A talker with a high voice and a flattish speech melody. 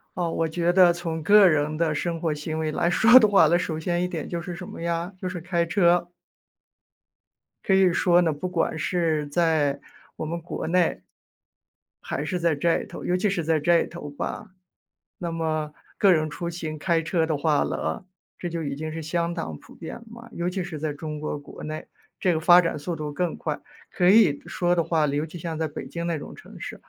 No: medium, 170 Hz; narrow, 2.1 semitones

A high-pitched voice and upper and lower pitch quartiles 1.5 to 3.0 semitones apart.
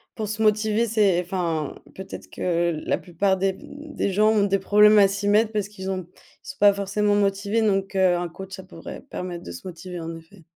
Yes: high, 195 Hz; narrow, 2.5 semitones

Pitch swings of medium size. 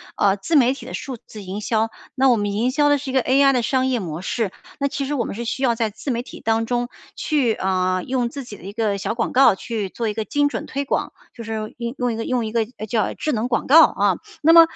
Yes: average, 3.7 semitones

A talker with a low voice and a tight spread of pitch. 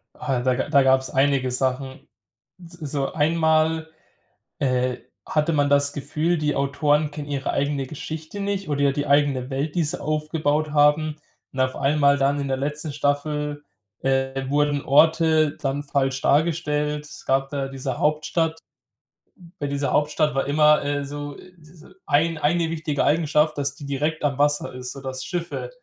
No: medium, 145 Hz; narrow, 2.0 semitones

